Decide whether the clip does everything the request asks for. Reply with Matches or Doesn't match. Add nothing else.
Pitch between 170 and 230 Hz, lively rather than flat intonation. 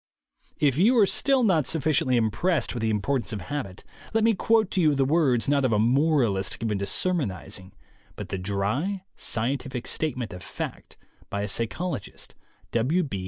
Doesn't match